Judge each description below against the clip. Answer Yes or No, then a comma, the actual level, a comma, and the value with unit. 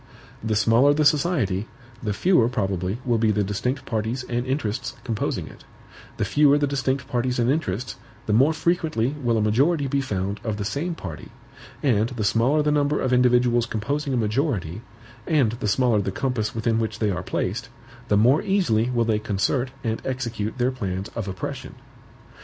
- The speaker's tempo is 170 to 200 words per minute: Yes, average, 180 wpm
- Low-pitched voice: Yes, low, 120 Hz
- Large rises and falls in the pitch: No, average, 4.4 semitones